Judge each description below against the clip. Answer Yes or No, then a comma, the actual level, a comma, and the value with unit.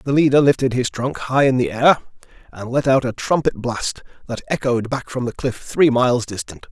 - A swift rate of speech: Yes, fast, 215 wpm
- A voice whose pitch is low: Yes, low, 125 Hz